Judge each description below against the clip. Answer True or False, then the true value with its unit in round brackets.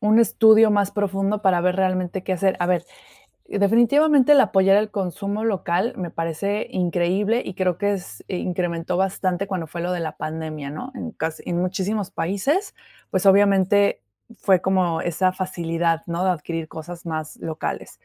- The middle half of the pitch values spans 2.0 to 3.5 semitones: True (2.9 semitones)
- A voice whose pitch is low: False (185 Hz)